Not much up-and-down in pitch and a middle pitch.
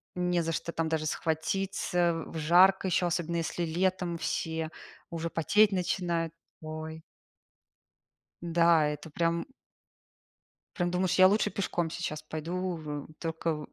Yes: narrow, 1.9 semitones; medium, 170 Hz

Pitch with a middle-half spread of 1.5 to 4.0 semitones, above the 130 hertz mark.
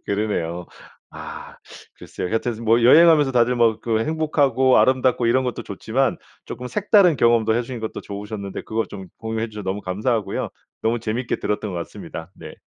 No: average, 3.4 semitones; low, 115 Hz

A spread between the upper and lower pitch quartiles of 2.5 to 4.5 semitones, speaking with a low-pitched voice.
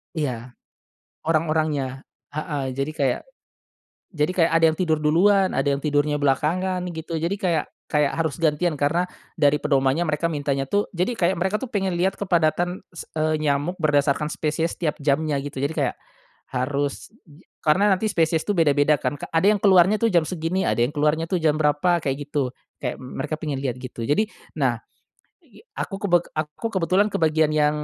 No: average, 3.3 semitones; medium, 155 Hz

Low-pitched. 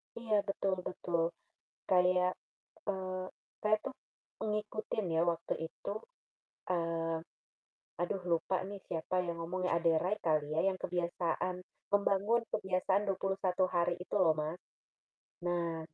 No: medium, 180 Hz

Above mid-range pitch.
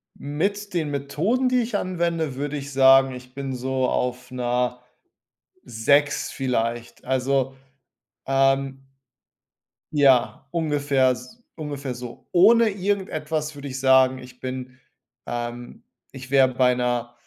No: low, 135 Hz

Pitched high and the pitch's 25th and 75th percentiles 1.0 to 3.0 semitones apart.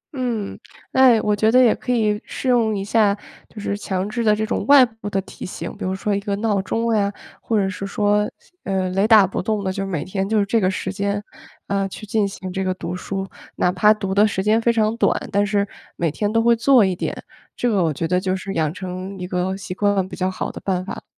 Yes: high, 200 Hz; narrow, 2.4 semitones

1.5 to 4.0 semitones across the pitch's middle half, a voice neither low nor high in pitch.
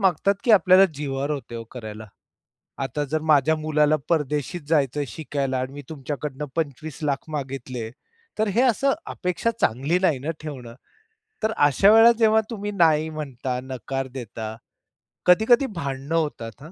No: average, 4.6 semitones; medium, 150 Hz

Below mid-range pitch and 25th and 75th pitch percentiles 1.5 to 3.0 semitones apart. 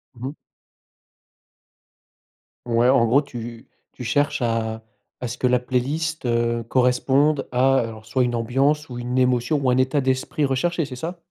Yes: low, 125 Hz; average, 2.7 semitones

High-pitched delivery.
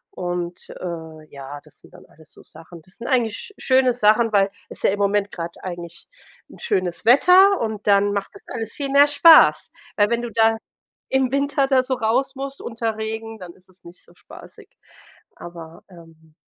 Yes: high, 210 Hz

